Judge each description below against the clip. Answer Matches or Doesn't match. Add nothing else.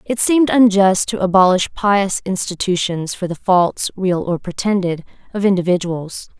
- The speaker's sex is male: Doesn't match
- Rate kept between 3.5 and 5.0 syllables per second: Matches